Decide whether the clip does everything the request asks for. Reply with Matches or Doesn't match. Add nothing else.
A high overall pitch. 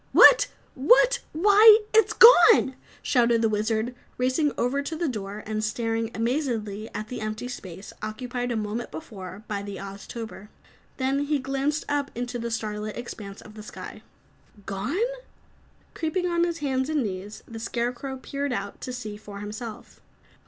Matches